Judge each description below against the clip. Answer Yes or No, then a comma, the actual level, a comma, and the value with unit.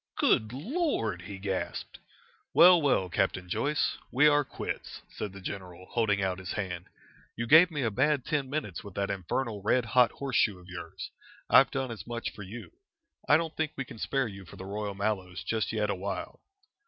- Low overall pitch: Yes, low, 110 Hz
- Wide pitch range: Yes, wide, 6.0 semitones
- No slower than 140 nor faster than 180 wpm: No, average, 190 wpm